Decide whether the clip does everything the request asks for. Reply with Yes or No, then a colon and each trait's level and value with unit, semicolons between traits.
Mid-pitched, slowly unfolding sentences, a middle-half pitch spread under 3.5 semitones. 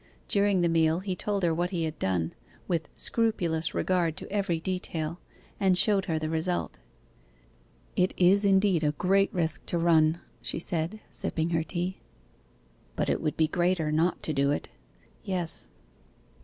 No: medium, 170 Hz; average, 165 wpm; average, 2.7 semitones